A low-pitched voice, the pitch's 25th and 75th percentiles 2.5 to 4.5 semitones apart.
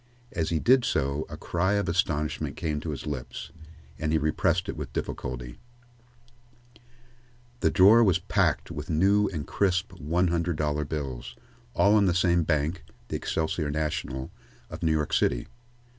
Yes: very low, 80 Hz; average, 3.6 semitones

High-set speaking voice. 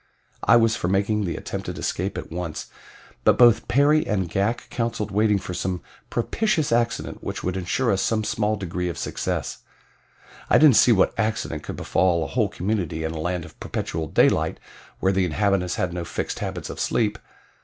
No: low, 100 Hz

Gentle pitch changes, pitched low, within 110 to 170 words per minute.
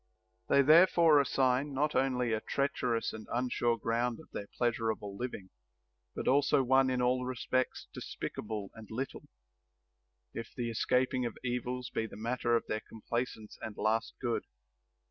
Yes: narrow, 2.3 semitones; low, 125 Hz; average, 155 wpm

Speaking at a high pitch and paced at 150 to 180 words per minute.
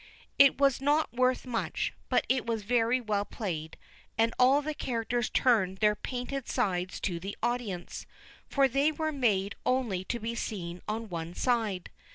Yes: high, 230 Hz; average, 165 wpm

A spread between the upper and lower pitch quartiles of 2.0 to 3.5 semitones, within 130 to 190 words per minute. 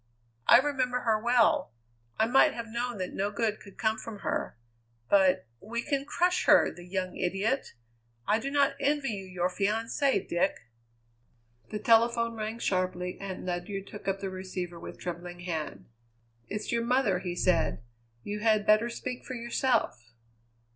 No: average, 4.4 semitones; average, 160 wpm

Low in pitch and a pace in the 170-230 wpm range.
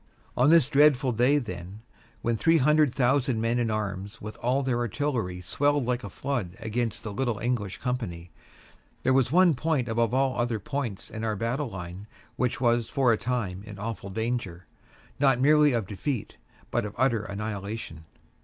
Yes: low, 120 Hz; average, 175 wpm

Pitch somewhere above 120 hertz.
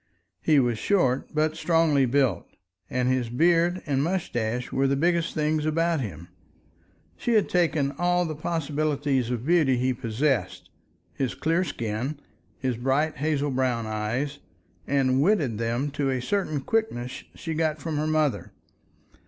Yes: medium, 140 Hz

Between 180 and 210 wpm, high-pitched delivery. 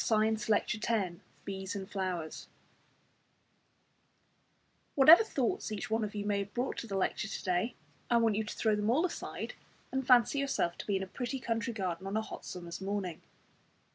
Yes: average, 190 wpm; high, 210 Hz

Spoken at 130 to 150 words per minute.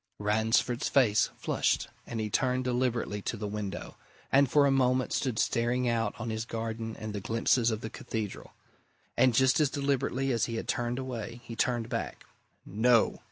No: average, 175 wpm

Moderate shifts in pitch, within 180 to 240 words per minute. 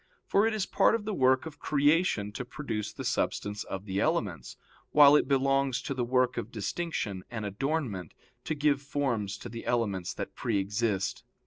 No: wide, 6.1 semitones; average, 185 wpm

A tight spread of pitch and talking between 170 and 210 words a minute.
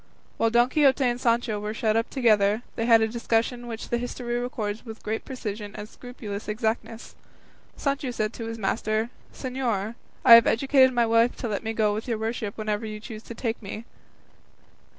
Yes: narrow, 2.0 semitones; average, 190 wpm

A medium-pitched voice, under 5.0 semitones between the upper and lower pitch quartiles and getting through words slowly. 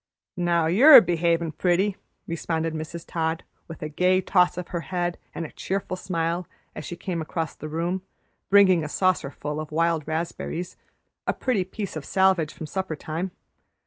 No: medium, 170 Hz; narrow, 2.5 semitones; average, 165 wpm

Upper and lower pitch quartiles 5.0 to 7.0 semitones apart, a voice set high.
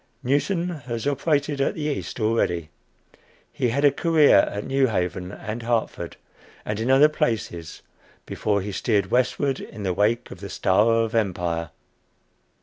No: wide, 5.5 semitones; low, 115 Hz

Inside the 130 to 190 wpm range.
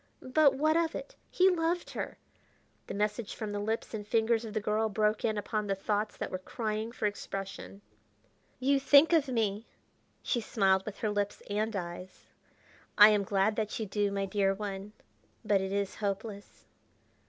Yes: average, 175 wpm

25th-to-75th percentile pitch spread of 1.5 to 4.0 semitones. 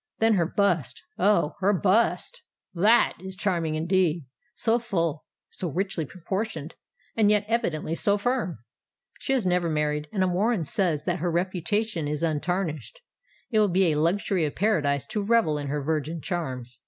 No: average, 4.8 semitones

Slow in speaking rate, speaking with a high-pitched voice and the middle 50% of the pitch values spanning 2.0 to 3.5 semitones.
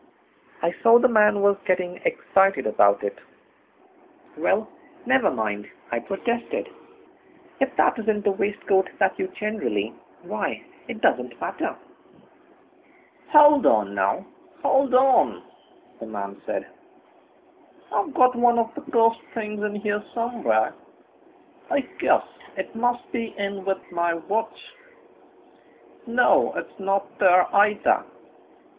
No: slow, 125 wpm; high, 210 Hz; average, 4.1 semitones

